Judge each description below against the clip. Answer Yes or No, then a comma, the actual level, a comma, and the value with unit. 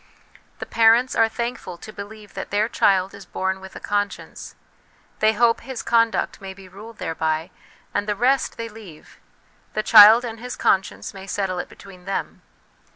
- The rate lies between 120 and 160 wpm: No, average, 170 wpm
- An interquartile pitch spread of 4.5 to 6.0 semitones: No, average, 3.0 semitones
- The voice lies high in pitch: Yes, high, 205 Hz